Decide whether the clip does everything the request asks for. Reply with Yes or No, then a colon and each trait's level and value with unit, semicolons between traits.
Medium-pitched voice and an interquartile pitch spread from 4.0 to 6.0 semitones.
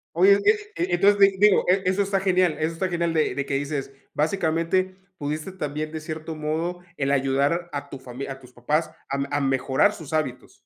Yes: medium, 160 Hz; average, 4.7 semitones